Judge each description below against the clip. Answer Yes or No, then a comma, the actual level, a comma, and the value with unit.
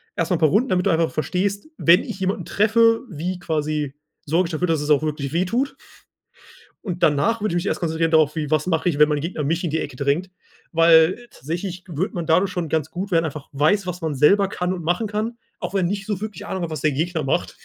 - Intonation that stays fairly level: No, average, 3.5 semitones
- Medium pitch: Yes, medium, 170 Hz